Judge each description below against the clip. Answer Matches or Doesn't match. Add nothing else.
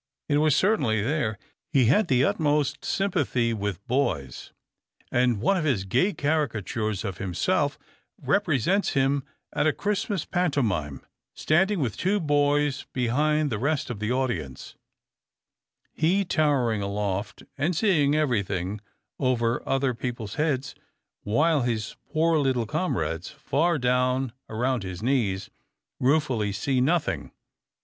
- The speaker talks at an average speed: Doesn't match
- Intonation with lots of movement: Matches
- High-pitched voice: Doesn't match